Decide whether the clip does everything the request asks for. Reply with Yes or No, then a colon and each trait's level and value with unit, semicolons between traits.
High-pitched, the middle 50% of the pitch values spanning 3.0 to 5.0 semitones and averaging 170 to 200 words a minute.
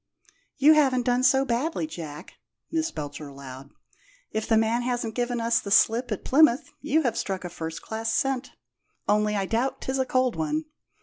Yes: high, 235 Hz; average, 4.1 semitones; average, 180 wpm